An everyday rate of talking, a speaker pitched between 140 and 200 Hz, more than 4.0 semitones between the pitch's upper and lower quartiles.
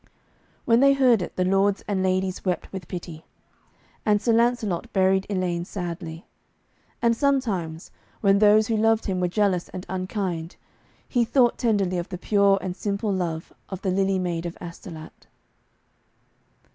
No: average, 155 wpm; high, 190 Hz; average, 3.1 semitones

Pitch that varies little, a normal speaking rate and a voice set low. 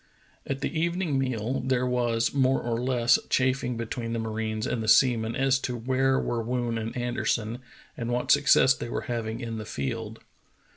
Yes: narrow, 2.3 semitones; average, 185 wpm; low, 120 Hz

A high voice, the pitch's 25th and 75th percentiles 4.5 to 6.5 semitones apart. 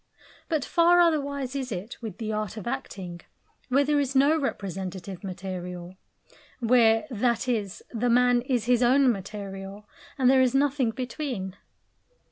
Yes: high, 240 Hz; average, 5.3 semitones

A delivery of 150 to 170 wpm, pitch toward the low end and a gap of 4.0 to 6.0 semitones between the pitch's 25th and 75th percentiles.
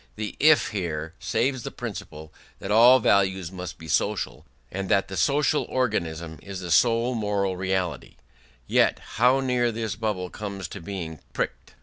Yes: average, 155 wpm; low, 100 Hz; average, 4.4 semitones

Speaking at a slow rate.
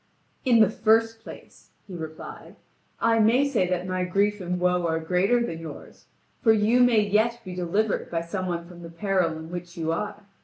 No: average, 195 wpm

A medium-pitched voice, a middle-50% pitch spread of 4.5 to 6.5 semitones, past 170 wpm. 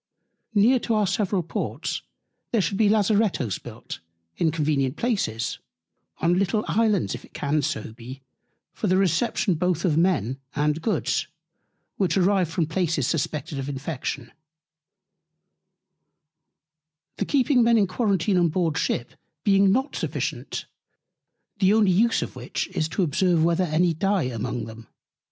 No: medium, 175 Hz; average, 5.2 semitones; average, 145 wpm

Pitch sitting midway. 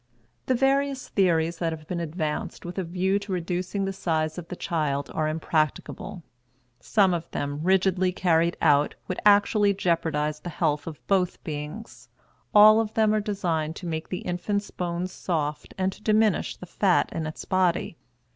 Yes: medium, 175 Hz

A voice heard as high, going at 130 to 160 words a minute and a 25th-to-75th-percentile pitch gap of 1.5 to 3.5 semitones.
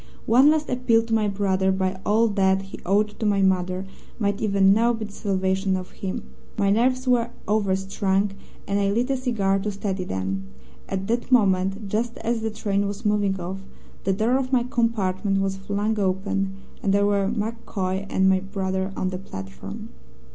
No: high, 200 Hz; average, 185 wpm; narrow, 2.6 semitones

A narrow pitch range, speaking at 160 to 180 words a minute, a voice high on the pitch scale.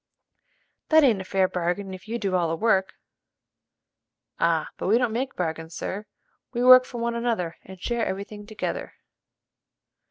No: average, 4.4 semitones; average, 165 wpm; high, 200 Hz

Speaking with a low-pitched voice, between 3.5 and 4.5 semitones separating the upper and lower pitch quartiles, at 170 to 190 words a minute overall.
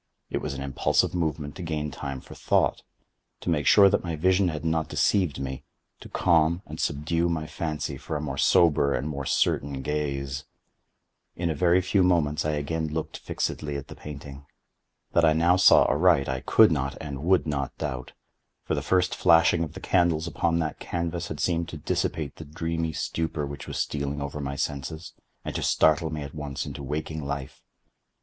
No: very low, 75 Hz; average, 2.8 semitones; average, 185 wpm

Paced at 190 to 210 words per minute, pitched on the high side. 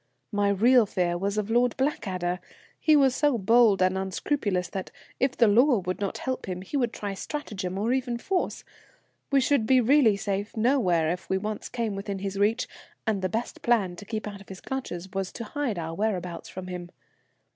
Yes: average, 200 wpm; high, 205 Hz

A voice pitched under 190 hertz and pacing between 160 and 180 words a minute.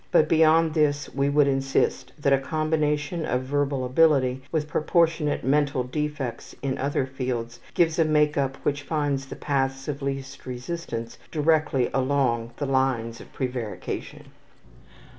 No: medium, 140 Hz; average, 140 wpm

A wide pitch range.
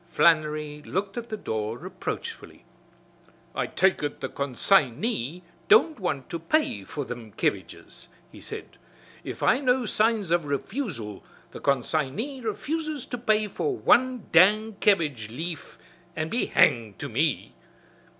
Yes: wide, 8.3 semitones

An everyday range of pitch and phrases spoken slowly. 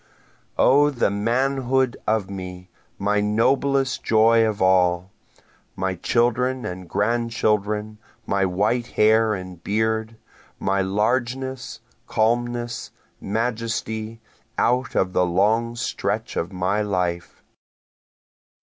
Yes: average, 3.6 semitones; slow, 105 wpm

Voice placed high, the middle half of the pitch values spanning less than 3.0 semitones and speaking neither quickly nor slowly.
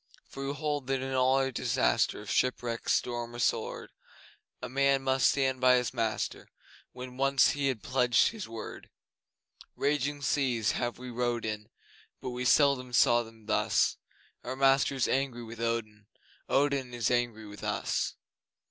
No: low, 125 Hz; narrow, 2.4 semitones; average, 155 wpm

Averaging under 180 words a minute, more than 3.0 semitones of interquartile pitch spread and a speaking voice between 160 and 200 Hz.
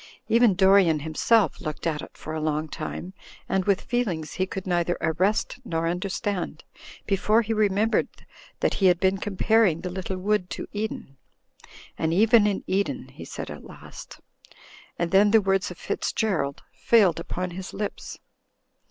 Yes: average, 160 wpm; average, 3.6 semitones; high, 190 Hz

